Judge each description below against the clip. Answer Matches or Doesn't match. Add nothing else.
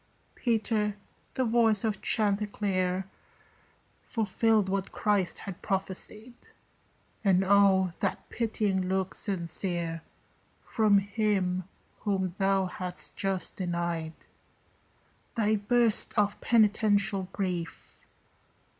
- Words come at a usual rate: Doesn't match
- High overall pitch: Matches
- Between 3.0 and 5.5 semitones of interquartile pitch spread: Doesn't match